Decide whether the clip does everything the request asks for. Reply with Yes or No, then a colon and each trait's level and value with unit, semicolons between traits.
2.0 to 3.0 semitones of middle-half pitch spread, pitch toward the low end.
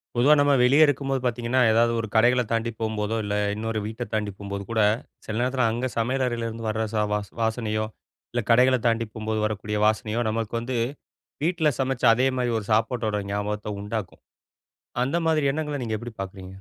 Yes: average, 2.7 semitones; low, 115 Hz